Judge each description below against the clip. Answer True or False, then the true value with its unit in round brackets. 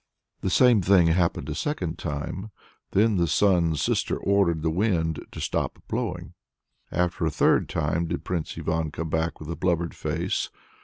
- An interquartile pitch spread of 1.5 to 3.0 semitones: True (2.6 semitones)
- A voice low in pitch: True (85 Hz)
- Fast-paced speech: False (165 wpm)